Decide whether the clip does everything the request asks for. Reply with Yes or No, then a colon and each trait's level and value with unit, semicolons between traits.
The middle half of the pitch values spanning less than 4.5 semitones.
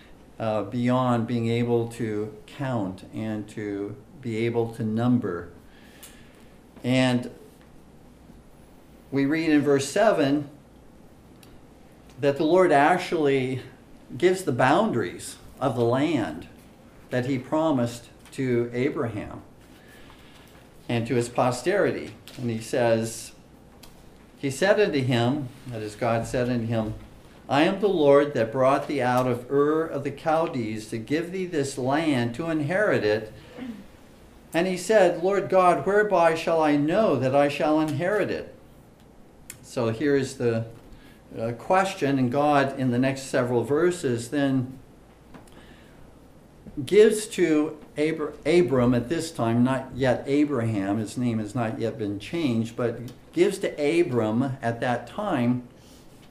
Yes: average, 4.1 semitones